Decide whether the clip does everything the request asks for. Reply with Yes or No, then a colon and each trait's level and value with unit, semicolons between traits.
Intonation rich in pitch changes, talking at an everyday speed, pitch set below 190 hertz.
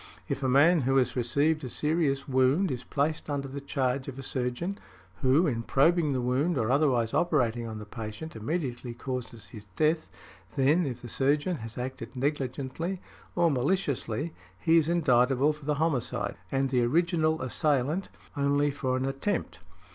No: average, 3.8 semitones; average, 165 wpm; low, 135 Hz